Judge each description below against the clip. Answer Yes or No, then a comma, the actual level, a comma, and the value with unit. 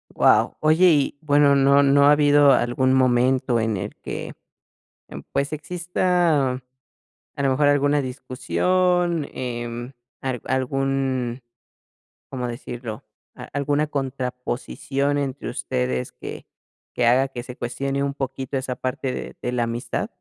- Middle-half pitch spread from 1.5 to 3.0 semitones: Yes, narrow, 2.4 semitones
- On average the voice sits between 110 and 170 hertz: Yes, low, 135 Hz